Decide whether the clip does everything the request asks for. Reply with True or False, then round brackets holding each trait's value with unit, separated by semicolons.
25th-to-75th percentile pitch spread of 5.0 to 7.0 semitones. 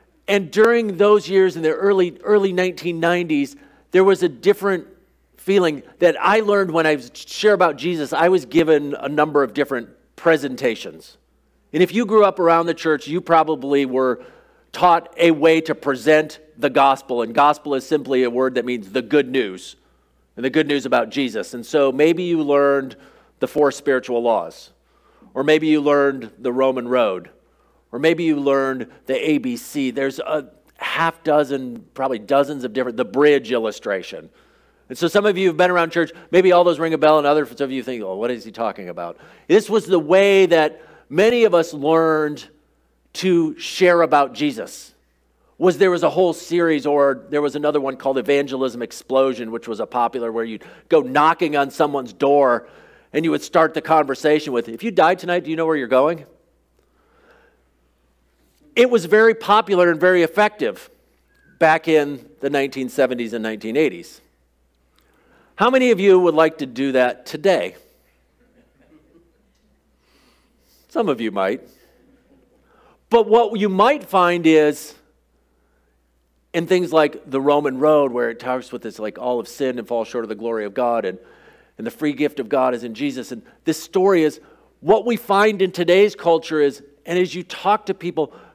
True (5.3 semitones)